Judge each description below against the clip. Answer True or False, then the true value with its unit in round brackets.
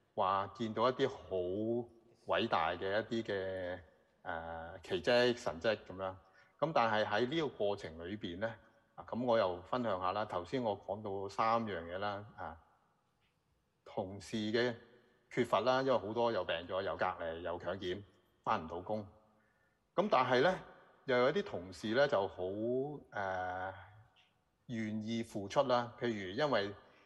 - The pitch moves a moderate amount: True (4.1 semitones)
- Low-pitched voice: True (110 Hz)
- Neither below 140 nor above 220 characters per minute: True (210 characters per minute)